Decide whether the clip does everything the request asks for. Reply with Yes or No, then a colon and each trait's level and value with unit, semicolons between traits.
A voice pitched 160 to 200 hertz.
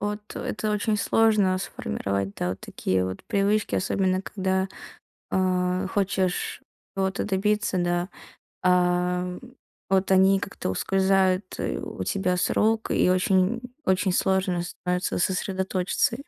Yes: high, 190 Hz